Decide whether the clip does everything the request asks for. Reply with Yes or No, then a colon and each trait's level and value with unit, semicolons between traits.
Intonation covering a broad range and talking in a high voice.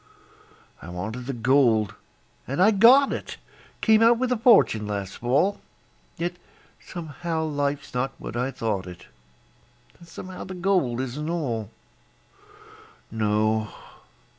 No: wide, 8.2 semitones; low, 135 Hz